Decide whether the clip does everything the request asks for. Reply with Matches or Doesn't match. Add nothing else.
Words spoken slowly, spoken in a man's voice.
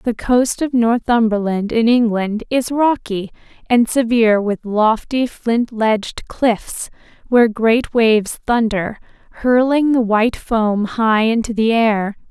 Doesn't match